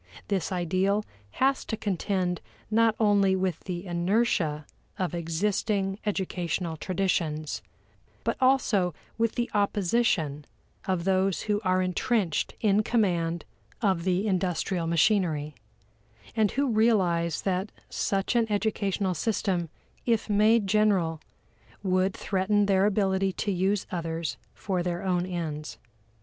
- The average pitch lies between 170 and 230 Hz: Yes, high, 190 Hz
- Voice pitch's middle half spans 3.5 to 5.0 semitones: No, average, 3.1 semitones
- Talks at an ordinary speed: No, slow, 120 wpm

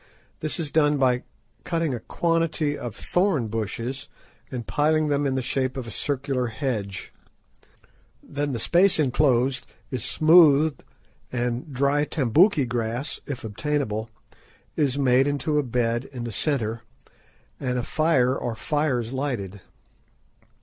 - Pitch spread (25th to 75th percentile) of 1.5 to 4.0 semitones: Yes, average, 3.6 semitones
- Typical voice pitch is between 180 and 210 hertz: No, low, 135 Hz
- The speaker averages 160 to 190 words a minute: No, slow, 135 wpm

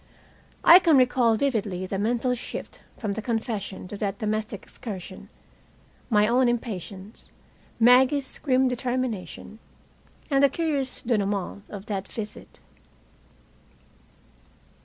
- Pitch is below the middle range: No, high, 225 Hz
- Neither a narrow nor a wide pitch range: Yes, average, 4.0 semitones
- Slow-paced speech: Yes, slow, 110 wpm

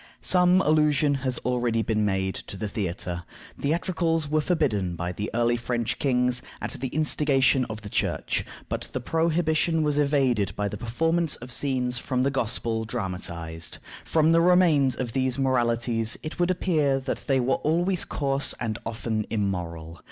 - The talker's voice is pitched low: Yes, low, 130 Hz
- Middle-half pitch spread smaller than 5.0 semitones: No, wide, 5.5 semitones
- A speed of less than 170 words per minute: Yes, average, 160 wpm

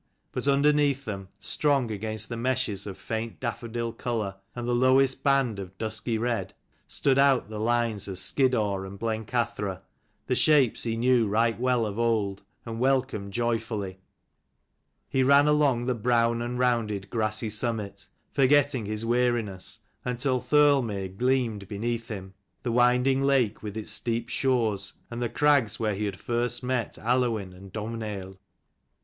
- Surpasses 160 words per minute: No, average, 150 wpm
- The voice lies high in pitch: No, low, 115 Hz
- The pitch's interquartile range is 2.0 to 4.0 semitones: Yes, average, 3.2 semitones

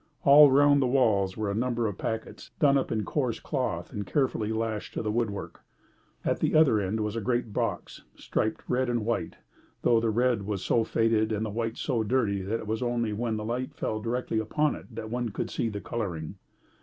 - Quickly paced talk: Yes, fast, 215 wpm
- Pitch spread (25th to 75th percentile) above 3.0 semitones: No, average, 2.7 semitones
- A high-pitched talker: No, low, 115 Hz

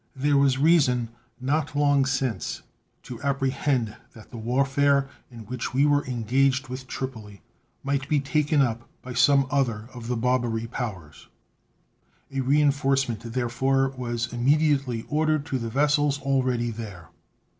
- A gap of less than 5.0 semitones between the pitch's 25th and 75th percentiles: Yes, average, 2.9 semitones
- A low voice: Yes, low, 130 Hz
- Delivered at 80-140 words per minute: Yes, slow, 135 wpm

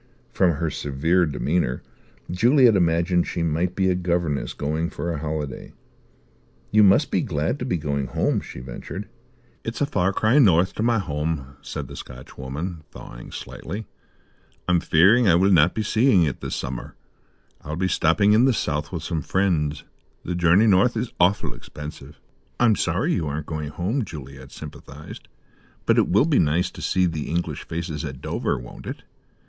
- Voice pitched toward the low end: Yes, very low, 85 Hz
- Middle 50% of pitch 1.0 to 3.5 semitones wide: No, average, 4.4 semitones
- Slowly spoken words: No, average, 175 wpm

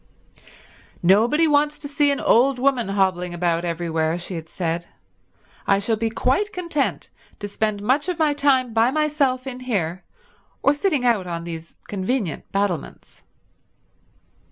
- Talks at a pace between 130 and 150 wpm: Yes, average, 145 wpm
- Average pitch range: No, wide, 7.8 semitones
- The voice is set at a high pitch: Yes, high, 225 Hz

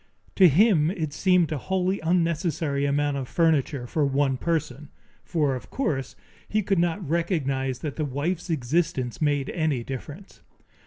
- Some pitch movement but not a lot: Yes, average, 3.7 semitones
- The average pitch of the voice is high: No, medium, 155 Hz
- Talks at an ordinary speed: Yes, average, 150 wpm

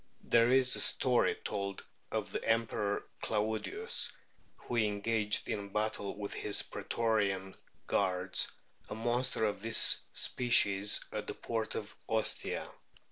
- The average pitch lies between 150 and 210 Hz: No, low, 110 Hz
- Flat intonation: Yes, narrow, 2.2 semitones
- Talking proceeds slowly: Yes, slow, 125 wpm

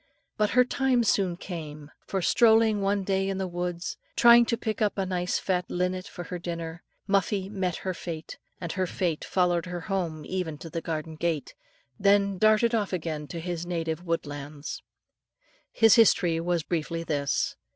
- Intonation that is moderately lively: Yes, average, 3.1 semitones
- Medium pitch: Yes, medium, 180 Hz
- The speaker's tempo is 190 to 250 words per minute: No, average, 170 wpm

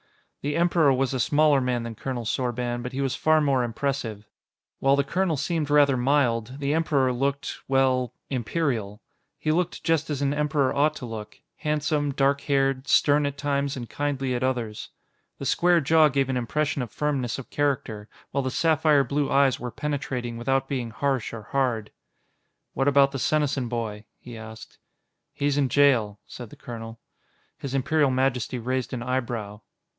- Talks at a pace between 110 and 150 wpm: No, average, 170 wpm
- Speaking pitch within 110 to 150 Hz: Yes, low, 135 Hz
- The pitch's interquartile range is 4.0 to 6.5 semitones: No, average, 3.0 semitones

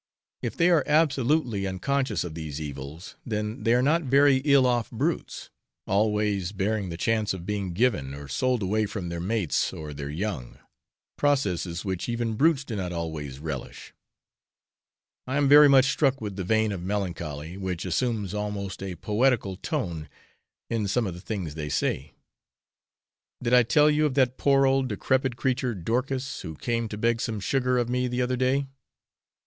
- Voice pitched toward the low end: Yes, low, 110 Hz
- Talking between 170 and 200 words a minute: Yes, average, 175 wpm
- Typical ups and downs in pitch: No, wide, 6.1 semitones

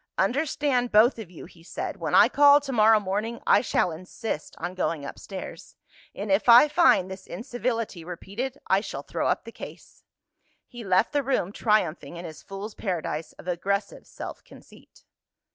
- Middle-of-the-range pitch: No, high, 205 Hz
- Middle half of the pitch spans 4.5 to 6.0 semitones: Yes, average, 5.0 semitones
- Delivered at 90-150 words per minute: No, average, 170 wpm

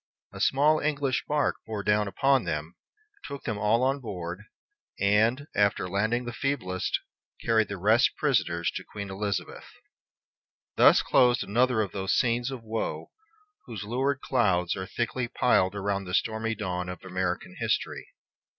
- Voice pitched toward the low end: Yes, low, 110 Hz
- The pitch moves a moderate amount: Yes, average, 4.5 semitones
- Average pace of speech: Yes, average, 150 wpm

